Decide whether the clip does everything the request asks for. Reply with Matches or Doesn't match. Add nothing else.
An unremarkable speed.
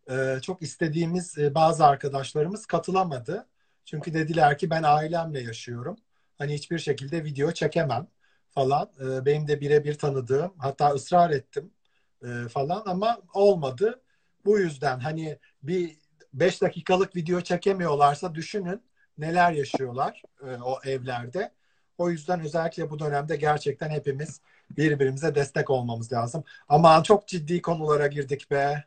Matches